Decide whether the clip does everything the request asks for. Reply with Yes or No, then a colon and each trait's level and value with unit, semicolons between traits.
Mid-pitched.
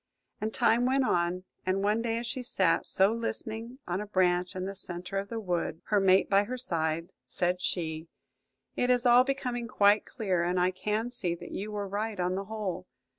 No: high, 200 Hz